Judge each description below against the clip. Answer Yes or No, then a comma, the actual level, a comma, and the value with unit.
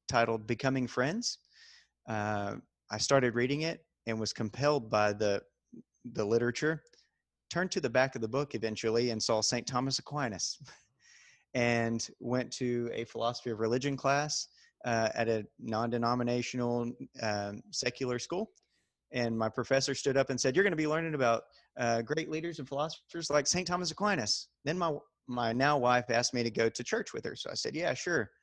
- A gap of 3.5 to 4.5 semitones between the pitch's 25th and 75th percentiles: Yes, average, 4.2 semitones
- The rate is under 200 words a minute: Yes, average, 175 wpm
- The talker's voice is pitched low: Yes, low, 125 Hz